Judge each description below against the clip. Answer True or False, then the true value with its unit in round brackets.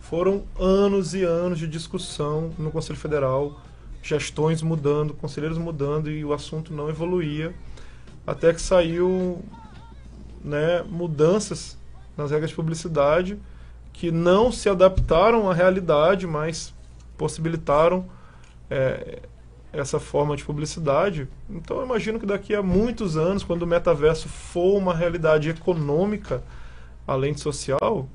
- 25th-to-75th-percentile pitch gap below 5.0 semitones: True (3.6 semitones)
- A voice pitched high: False (160 Hz)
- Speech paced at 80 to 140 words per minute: True (125 wpm)